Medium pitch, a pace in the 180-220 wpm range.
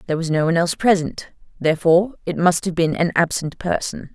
Yes: medium, 170 Hz; average, 200 wpm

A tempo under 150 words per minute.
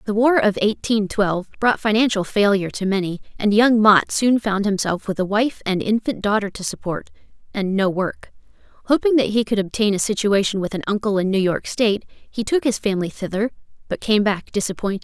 No: average, 200 wpm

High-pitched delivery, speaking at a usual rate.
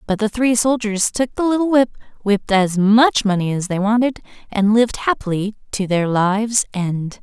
Yes: high, 215 Hz; average, 185 wpm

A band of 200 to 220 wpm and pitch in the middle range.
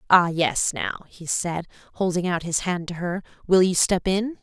Yes: fast, 205 wpm; medium, 180 Hz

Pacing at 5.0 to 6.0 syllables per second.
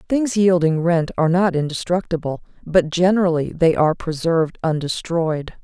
Yes: 5.2 syllables/s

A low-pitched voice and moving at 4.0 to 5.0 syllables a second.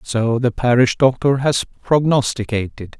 Yes: low, 125 Hz; 4.4 syllables/s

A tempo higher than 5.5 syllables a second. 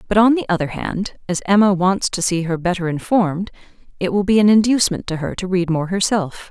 Yes: 5.8 syllables/s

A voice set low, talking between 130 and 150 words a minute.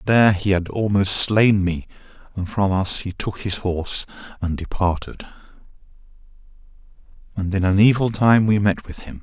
No: low, 100 Hz; average, 165 wpm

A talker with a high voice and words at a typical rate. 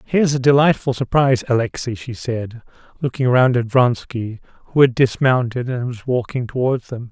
No: low, 125 Hz; average, 160 wpm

